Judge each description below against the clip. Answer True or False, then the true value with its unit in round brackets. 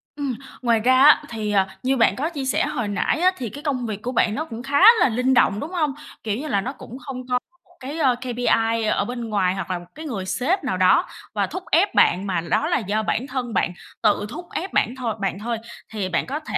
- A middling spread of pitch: True (4.7 semitones)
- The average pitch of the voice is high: True (245 Hz)